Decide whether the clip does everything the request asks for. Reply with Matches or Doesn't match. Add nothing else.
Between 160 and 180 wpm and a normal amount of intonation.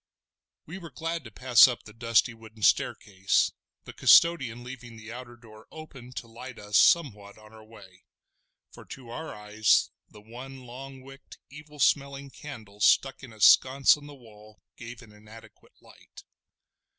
Matches